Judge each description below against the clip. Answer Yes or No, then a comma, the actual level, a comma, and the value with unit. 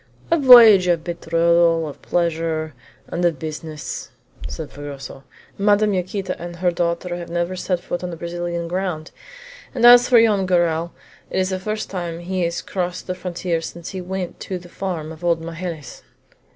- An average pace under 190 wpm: Yes, average, 170 wpm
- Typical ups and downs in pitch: No, narrow, 2.0 semitones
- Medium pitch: Yes, medium, 175 Hz